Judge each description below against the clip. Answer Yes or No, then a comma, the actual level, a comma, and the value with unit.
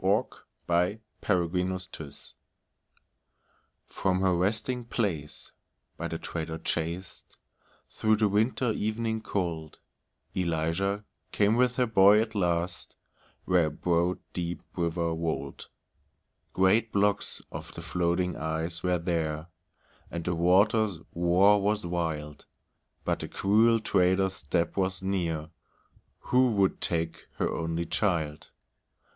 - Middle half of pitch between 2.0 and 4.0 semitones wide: Yes, average, 3.5 semitones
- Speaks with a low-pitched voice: Yes, very low, 90 Hz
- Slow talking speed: Yes, slow, 115 wpm